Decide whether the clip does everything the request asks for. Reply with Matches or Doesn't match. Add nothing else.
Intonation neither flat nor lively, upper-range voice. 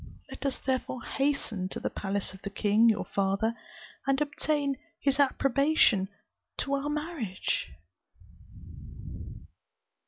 Doesn't match